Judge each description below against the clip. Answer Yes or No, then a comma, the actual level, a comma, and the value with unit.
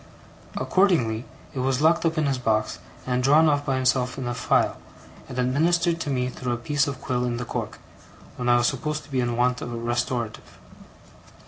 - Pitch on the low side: Yes, low, 130 Hz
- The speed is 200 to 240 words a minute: Yes, fast, 205 wpm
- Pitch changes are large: No, average, 3.1 semitones